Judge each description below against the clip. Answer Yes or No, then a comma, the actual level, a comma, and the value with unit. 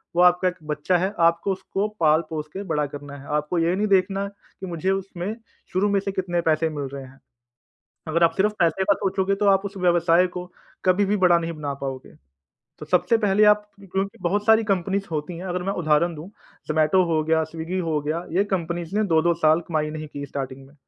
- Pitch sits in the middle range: Yes, medium, 175 Hz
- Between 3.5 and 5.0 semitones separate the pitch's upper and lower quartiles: Yes, average, 3.8 semitones